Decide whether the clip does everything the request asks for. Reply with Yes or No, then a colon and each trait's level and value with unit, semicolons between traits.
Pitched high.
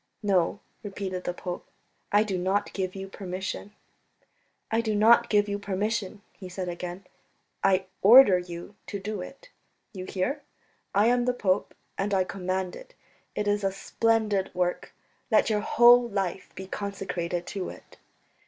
Yes: high, 195 Hz